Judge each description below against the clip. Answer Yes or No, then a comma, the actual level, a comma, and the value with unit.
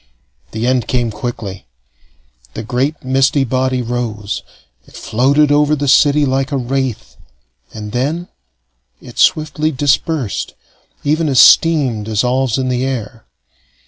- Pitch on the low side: Yes, low, 130 Hz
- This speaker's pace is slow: Yes, slow, 125 wpm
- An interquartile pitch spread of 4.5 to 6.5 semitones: No, average, 3.4 semitones